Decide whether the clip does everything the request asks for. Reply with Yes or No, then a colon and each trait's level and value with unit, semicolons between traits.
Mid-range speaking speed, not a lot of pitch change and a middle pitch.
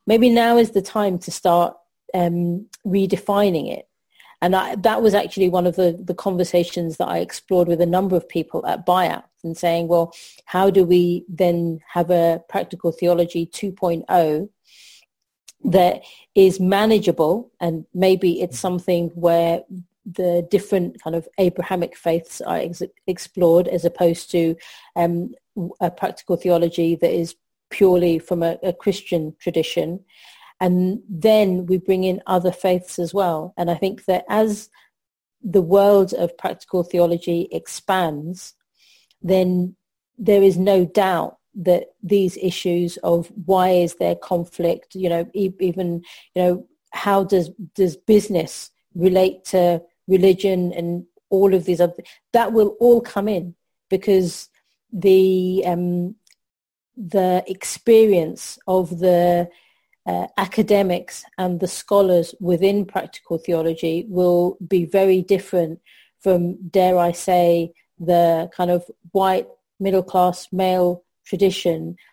No: slow, 130 wpm; narrow, 1.9 semitones; medium, 180 Hz